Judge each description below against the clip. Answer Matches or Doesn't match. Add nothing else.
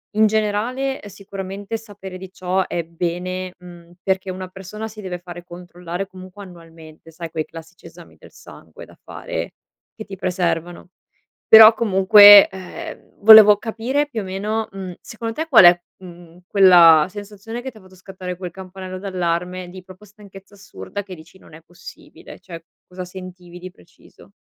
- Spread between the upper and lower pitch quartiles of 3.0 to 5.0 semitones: Doesn't match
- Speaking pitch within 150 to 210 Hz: Matches